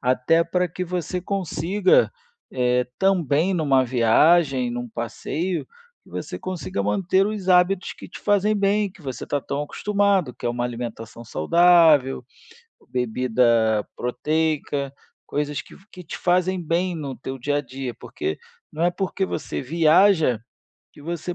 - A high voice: No, medium, 160 Hz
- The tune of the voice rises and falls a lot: Yes, wide, 6.2 semitones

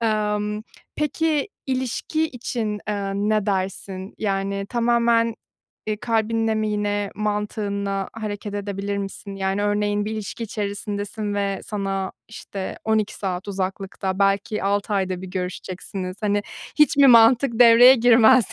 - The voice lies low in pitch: No, high, 205 Hz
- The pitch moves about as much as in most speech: No, narrow, 2.3 semitones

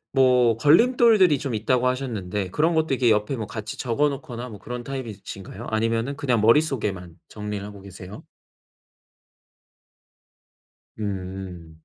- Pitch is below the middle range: Yes, low, 115 Hz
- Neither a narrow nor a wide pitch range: Yes, average, 4.9 semitones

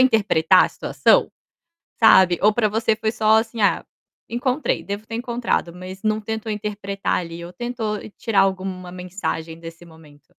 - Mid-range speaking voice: No, high, 205 Hz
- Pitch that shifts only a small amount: No, average, 3.6 semitones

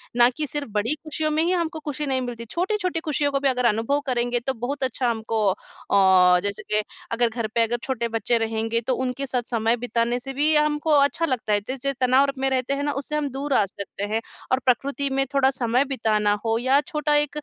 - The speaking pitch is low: No, very high, 260 Hz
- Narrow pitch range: No, average, 3.8 semitones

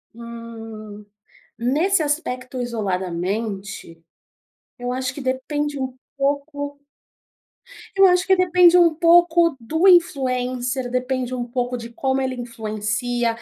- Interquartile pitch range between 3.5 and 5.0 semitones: Yes, average, 4.2 semitones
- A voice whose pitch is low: No, very high, 255 Hz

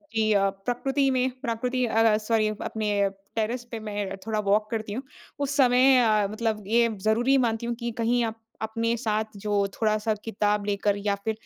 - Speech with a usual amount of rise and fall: No, narrow, 2.1 semitones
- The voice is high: Yes, high, 220 Hz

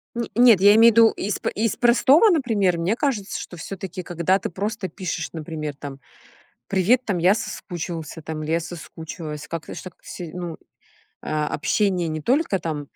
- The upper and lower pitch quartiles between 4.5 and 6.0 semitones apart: Yes, average, 5.1 semitones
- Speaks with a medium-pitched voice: Yes, medium, 180 Hz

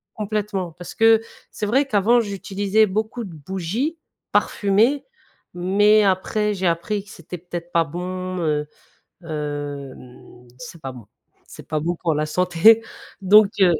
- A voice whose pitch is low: No, medium, 185 Hz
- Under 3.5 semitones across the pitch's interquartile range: No, average, 4.2 semitones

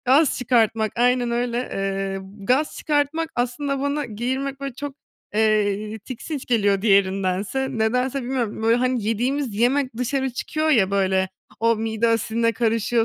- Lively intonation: No, average, 3.7 semitones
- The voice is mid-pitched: No, high, 235 Hz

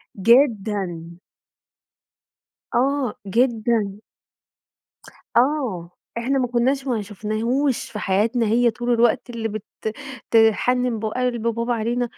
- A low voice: No, high, 235 Hz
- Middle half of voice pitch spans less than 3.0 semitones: Yes, narrow, 2.6 semitones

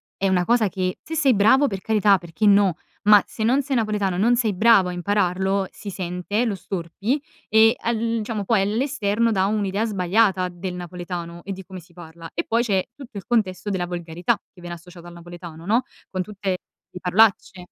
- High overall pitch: Yes, high, 195 Hz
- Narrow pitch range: No, average, 3.6 semitones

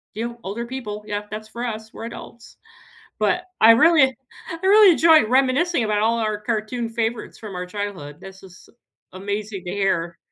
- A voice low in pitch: No, high, 220 Hz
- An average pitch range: Yes, average, 3.0 semitones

